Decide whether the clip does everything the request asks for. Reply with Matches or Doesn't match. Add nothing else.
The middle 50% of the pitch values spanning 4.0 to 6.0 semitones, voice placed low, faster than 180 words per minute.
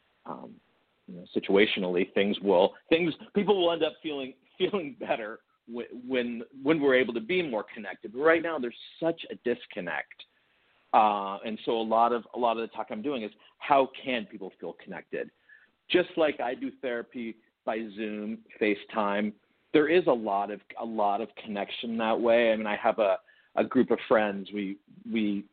Matches